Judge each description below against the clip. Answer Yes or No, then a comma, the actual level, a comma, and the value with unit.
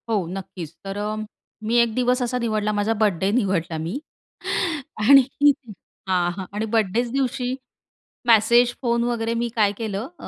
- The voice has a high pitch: Yes, high, 225 Hz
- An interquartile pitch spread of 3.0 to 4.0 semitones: Yes, average, 3.3 semitones